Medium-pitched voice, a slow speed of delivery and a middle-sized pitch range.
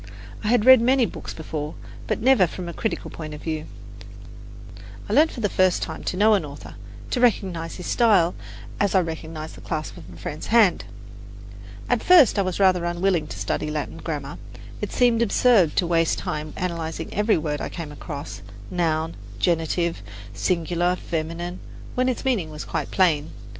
No: medium, 175 Hz; average, 175 wpm; average, 4.7 semitones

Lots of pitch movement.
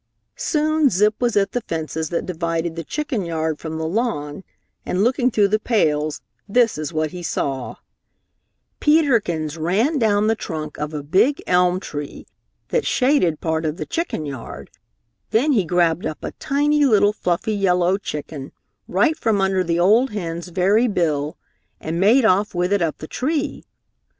Yes: wide, 6.1 semitones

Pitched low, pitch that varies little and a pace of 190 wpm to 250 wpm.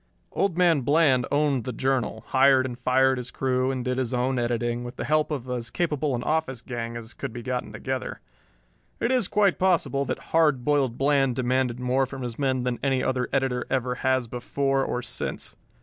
Yes: low, 130 Hz; narrow, 2.0 semitones; average, 195 wpm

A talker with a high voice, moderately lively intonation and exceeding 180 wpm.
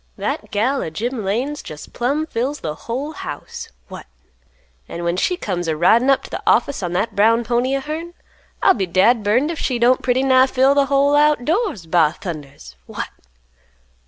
No: high, 245 Hz; wide, 6.8 semitones; average, 190 wpm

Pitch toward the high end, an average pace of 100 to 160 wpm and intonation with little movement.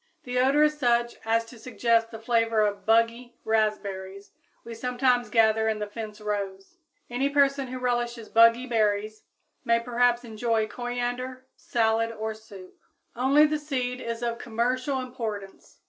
Yes: high, 230 Hz; average, 145 wpm; narrow, 2.3 semitones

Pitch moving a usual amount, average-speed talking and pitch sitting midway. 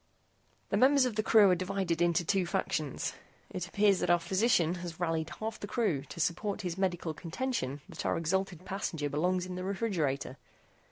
Yes: average, 3.1 semitones; average, 180 wpm; medium, 180 Hz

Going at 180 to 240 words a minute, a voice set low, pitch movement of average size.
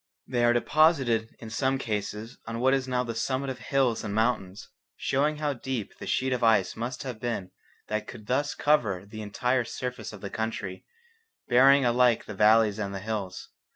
Yes: average, 190 wpm; low, 120 Hz; average, 3.4 semitones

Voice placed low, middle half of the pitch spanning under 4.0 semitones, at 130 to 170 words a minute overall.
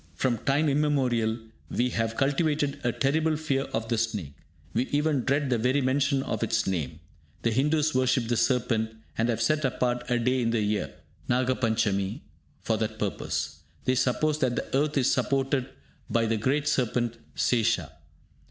Yes: low, 125 Hz; average, 3.6 semitones; average, 165 wpm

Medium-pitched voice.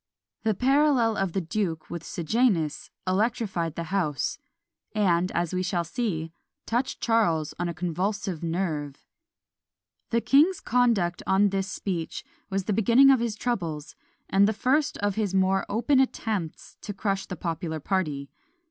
No: high, 195 Hz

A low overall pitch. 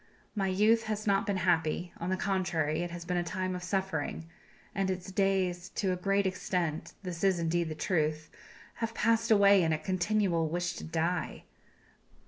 No: medium, 185 Hz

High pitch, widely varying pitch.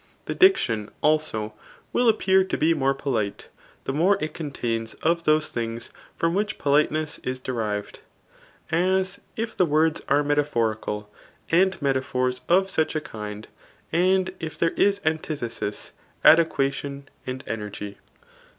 No: medium, 150 Hz; wide, 6.2 semitones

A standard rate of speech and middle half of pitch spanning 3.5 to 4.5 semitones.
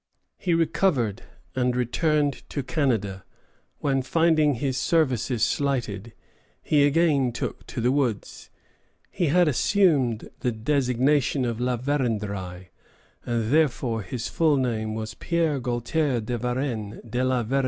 No: slow, 130 wpm; average, 4.1 semitones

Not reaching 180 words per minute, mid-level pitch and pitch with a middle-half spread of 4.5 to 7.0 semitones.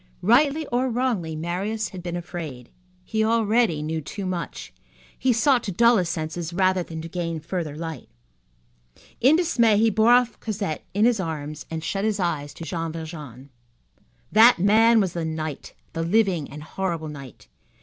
Yes: average, 170 wpm; medium, 180 Hz; wide, 5.6 semitones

